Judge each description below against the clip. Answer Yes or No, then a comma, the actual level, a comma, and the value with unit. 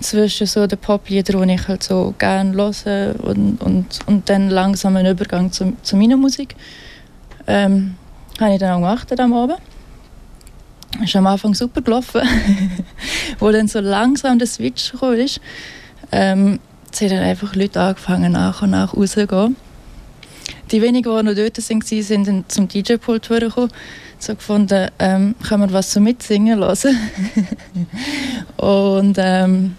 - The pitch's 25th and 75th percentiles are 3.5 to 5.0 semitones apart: No, average, 2.8 semitones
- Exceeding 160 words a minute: No, average, 155 wpm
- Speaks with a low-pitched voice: No, high, 205 Hz